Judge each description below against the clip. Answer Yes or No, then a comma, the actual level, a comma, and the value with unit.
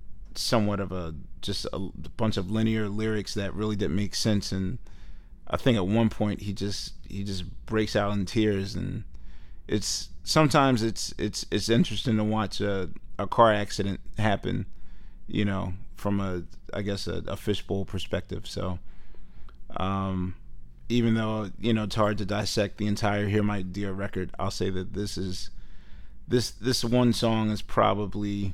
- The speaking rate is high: No, average, 165 wpm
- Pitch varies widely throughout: No, narrow, 2.5 semitones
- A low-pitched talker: Yes, low, 100 Hz